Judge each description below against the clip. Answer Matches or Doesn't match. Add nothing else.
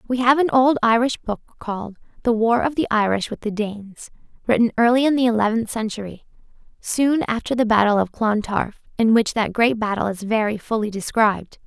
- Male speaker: Doesn't match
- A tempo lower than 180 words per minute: Doesn't match